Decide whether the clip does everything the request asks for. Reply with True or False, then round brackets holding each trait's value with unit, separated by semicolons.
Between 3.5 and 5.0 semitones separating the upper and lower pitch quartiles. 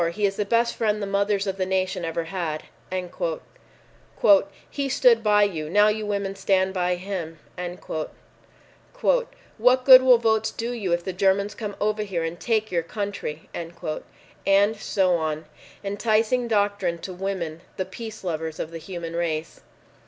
True (3.8 semitones)